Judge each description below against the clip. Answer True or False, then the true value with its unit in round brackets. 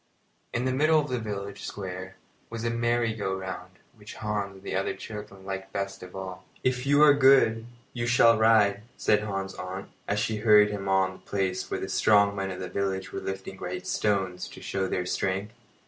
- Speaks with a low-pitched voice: True (100 Hz)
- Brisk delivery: True (210 wpm)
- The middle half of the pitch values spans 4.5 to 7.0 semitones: False (2.9 semitones)